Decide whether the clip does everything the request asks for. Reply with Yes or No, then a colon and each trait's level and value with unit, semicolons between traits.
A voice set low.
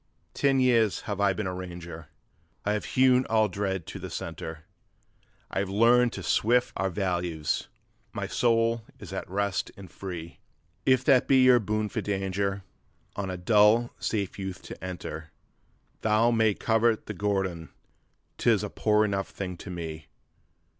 Yes: low, 100 Hz